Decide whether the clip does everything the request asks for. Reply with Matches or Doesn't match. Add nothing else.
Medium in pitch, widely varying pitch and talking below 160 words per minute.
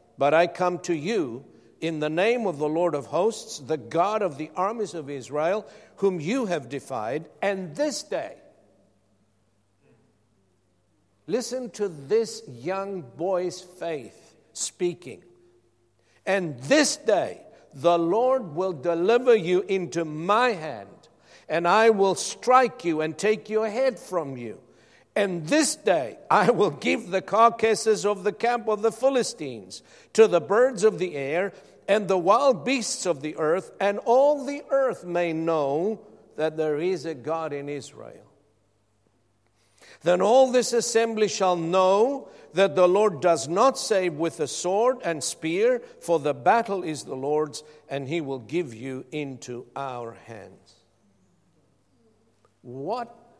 Matches